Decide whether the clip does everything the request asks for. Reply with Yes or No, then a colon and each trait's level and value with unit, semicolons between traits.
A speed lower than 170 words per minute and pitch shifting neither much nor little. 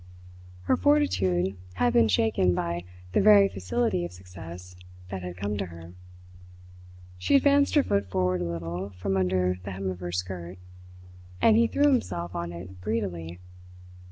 No: average, 155 wpm; narrow, 2.3 semitones